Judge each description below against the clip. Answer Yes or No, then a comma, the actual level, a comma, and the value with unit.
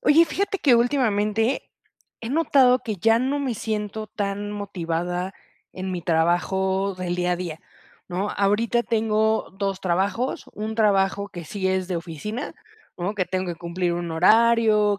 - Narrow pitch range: No, average, 3.7 semitones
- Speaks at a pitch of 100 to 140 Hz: No, high, 200 Hz